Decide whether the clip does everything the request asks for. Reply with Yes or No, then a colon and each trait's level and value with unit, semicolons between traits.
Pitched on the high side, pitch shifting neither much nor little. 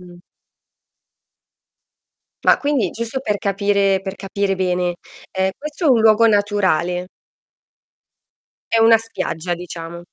Yes: high, 195 Hz; average, 3.9 semitones